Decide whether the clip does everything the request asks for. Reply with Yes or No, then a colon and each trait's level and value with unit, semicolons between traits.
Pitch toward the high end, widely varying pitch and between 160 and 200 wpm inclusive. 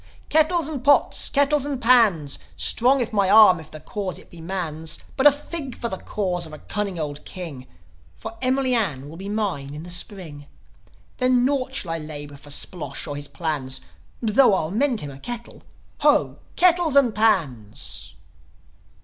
Yes: high, 195 Hz; wide, 8.5 semitones; average, 175 wpm